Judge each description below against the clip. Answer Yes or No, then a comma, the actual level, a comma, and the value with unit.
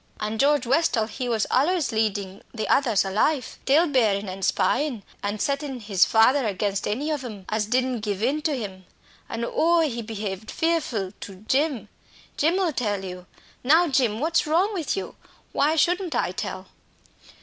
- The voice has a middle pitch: No, high, 245 Hz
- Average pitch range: No, wide, 6.2 semitones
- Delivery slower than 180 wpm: Yes, average, 170 wpm